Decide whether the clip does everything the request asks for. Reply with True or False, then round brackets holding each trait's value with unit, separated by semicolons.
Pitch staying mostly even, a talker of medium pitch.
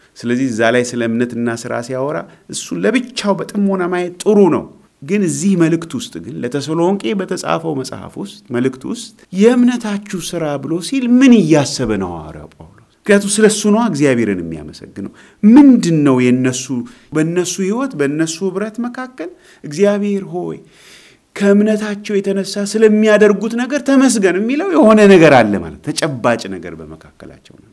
False (8.8 semitones; 180 Hz)